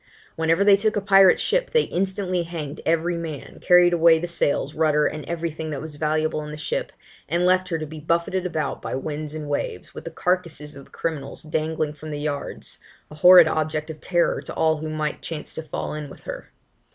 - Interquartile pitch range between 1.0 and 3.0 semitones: Yes, narrow, 2.5 semitones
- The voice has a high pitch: No, medium, 160 Hz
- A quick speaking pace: Yes, fast, 220 wpm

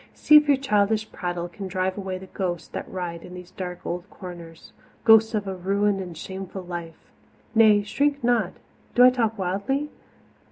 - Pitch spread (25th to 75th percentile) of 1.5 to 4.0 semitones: Yes, average, 3.7 semitones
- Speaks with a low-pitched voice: No, high, 195 Hz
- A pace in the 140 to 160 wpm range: No, average, 175 wpm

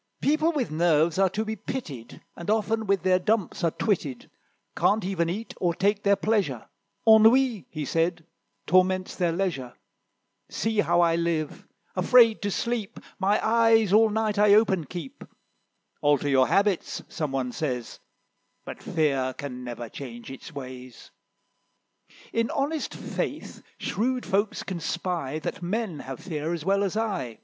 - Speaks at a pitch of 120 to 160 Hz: No, medium, 185 Hz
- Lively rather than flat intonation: Yes, wide, 6.2 semitones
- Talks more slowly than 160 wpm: Yes, average, 150 wpm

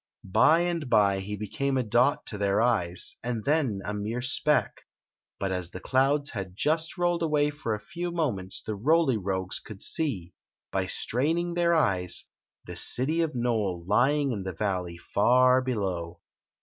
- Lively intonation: Yes, wide, 7.2 semitones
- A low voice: Yes, low, 120 Hz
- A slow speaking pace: No, average, 165 wpm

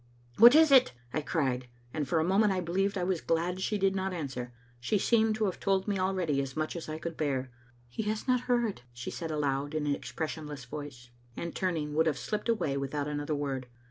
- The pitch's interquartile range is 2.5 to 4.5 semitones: No, average, 5.3 semitones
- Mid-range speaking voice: Yes, medium, 160 Hz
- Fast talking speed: Yes, fast, 235 wpm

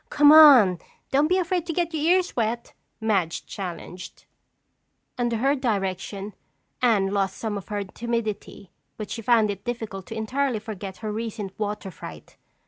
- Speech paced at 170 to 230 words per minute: No, average, 155 wpm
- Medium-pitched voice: No, high, 220 Hz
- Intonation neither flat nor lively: Yes, average, 4.4 semitones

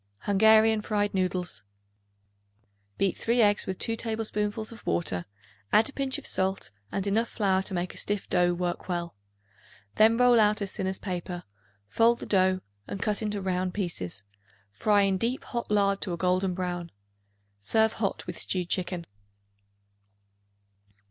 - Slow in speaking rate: No, average, 155 wpm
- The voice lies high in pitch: Yes, high, 195 Hz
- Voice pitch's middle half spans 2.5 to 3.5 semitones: Yes, average, 3.2 semitones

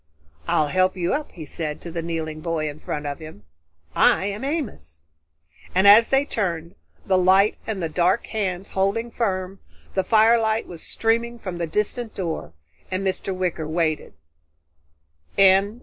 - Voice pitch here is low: No, medium, 185 Hz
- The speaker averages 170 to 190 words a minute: No, average, 155 wpm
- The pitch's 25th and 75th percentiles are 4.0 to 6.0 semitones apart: Yes, average, 4.8 semitones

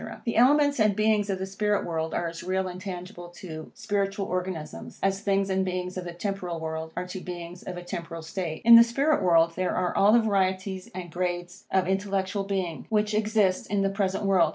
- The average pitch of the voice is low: No, high, 190 Hz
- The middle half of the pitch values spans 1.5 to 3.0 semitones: Yes, narrow, 2.4 semitones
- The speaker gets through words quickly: Yes, fast, 210 wpm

